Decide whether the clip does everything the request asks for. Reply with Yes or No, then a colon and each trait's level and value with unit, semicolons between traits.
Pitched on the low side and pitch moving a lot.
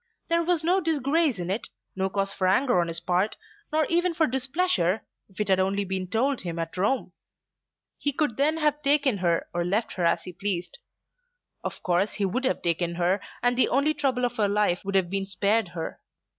No: high, 205 Hz; wide, 7.4 semitones